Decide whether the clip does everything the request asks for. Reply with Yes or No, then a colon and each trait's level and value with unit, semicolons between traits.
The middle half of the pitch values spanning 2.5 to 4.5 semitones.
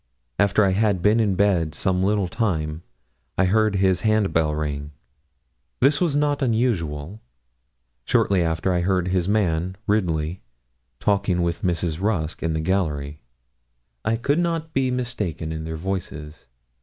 No: average, 5.0 semitones